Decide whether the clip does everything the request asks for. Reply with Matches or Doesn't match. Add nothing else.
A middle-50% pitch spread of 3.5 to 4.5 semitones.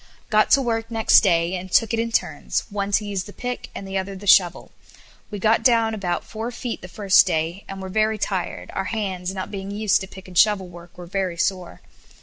Doesn't match